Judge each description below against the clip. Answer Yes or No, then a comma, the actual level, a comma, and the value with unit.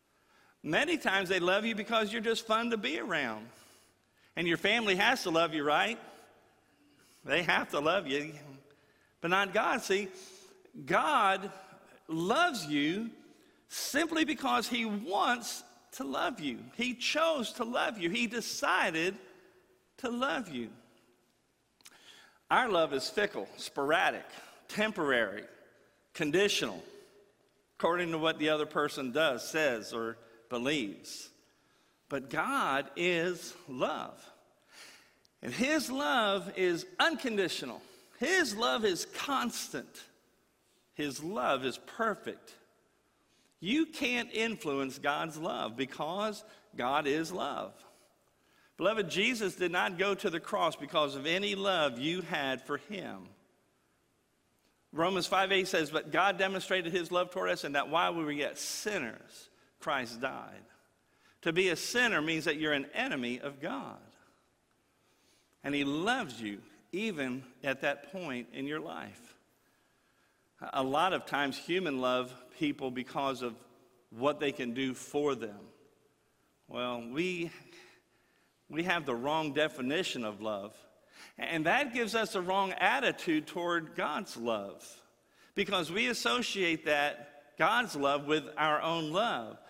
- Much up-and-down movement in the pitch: Yes, wide, 6.9 semitones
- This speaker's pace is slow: Yes, slow, 130 wpm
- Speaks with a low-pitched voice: No, medium, 175 Hz